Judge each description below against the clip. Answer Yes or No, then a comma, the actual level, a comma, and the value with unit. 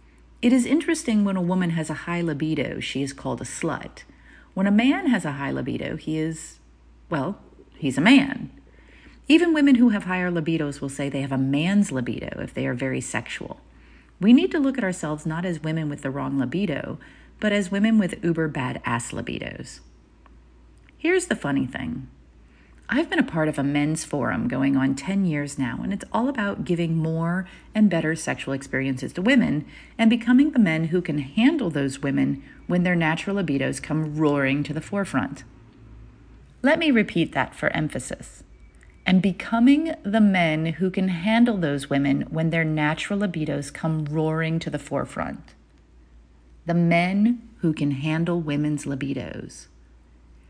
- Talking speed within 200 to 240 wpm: No, average, 170 wpm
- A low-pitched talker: No, medium, 160 Hz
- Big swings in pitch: Yes, wide, 6.5 semitones